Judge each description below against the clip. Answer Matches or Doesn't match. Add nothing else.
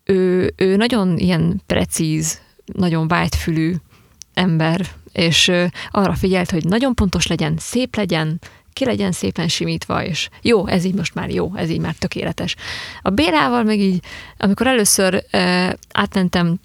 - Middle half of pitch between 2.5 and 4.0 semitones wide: Matches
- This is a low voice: Doesn't match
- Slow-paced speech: Doesn't match